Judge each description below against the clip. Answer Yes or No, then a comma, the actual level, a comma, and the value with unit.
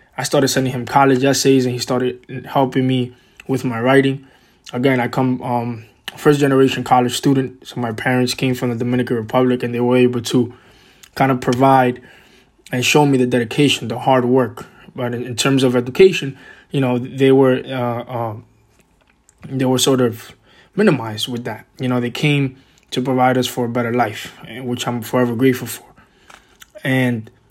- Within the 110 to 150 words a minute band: No, average, 175 wpm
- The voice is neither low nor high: No, low, 125 Hz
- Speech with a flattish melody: Yes, narrow, 1.5 semitones